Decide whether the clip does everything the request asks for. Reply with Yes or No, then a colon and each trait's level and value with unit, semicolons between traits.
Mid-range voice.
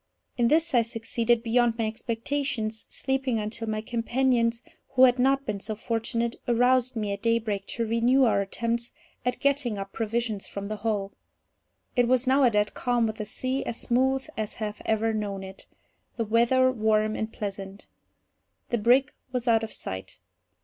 No: high, 230 Hz